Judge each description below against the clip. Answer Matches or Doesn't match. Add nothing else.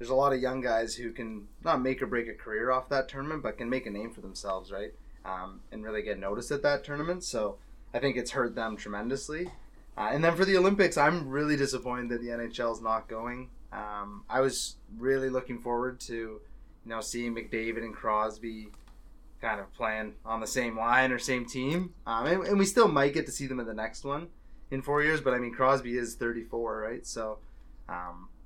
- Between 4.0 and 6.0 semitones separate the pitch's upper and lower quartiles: Doesn't match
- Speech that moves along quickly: Matches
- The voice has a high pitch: Doesn't match